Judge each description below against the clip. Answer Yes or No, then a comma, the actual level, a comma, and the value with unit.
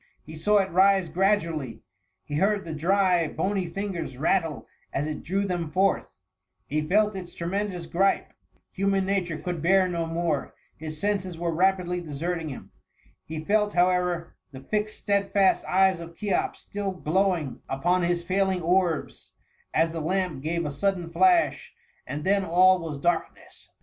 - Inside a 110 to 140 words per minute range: No, average, 165 wpm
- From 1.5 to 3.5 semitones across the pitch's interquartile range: Yes, average, 3.0 semitones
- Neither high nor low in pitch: Yes, medium, 180 Hz